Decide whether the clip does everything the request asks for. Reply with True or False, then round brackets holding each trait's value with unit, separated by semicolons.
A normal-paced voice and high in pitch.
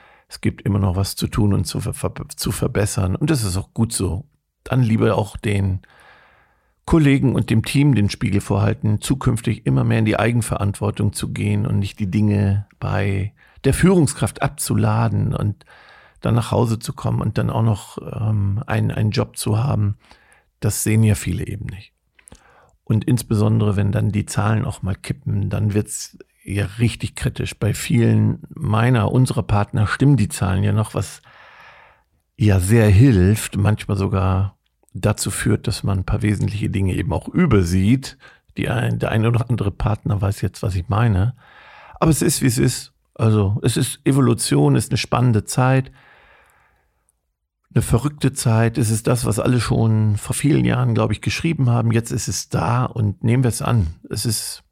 False (180 wpm; 110 Hz)